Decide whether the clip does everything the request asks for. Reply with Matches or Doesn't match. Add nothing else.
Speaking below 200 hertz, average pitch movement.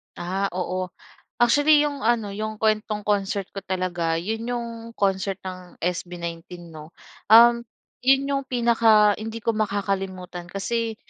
Doesn't match